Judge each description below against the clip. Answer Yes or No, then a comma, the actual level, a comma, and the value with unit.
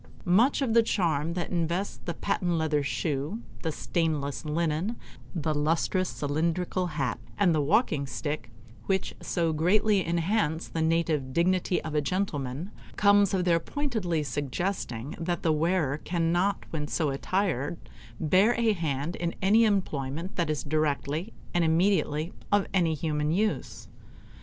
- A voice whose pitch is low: No, medium, 165 Hz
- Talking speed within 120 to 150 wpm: Yes, average, 140 wpm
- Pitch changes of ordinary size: Yes, average, 3.6 semitones